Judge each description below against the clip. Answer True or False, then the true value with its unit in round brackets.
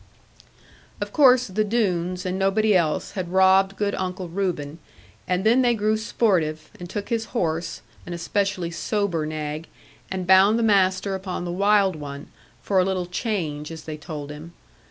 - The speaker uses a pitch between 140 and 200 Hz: True (185 Hz)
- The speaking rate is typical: True (165 wpm)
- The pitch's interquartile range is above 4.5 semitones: False (3.4 semitones)